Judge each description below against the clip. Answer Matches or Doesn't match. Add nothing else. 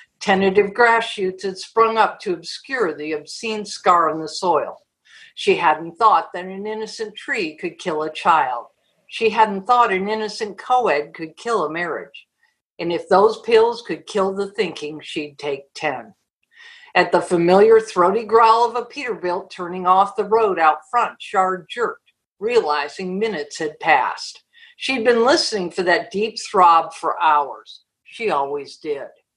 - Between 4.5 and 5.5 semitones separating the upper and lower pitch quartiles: Matches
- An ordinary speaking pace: Matches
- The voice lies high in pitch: Matches